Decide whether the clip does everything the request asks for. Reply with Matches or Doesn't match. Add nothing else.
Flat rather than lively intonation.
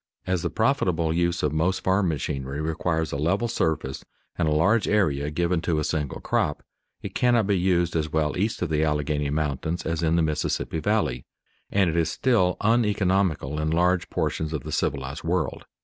Doesn't match